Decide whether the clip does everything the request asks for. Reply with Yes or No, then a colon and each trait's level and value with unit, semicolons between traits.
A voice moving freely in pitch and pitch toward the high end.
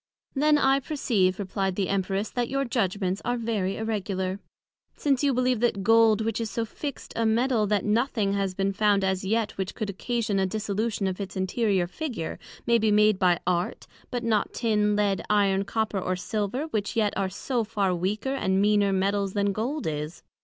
No: average, 3.1 semitones; high, 210 Hz